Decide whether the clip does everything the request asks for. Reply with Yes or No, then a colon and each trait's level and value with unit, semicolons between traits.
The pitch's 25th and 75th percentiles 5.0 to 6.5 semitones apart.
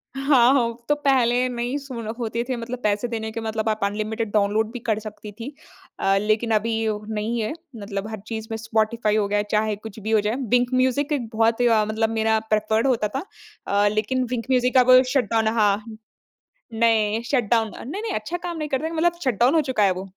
No: average, 2.7 semitones